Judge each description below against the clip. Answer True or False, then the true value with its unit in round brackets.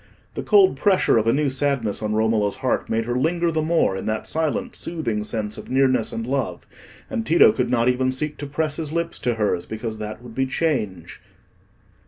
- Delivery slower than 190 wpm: False (205 wpm)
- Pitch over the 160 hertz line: False (130 Hz)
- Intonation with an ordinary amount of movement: False (6.0 semitones)